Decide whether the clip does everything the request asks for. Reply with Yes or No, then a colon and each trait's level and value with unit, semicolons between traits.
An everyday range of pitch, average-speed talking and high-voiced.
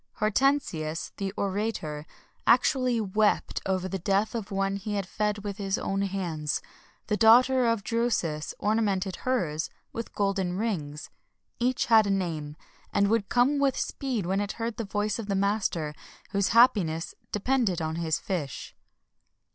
Yes: average, 3.9 semitones; average, 155 wpm; high, 200 Hz